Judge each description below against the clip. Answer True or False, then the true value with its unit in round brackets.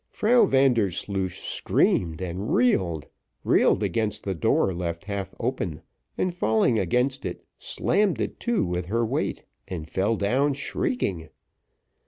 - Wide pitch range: True (6.2 semitones)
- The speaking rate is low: True (130 wpm)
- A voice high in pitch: False (100 Hz)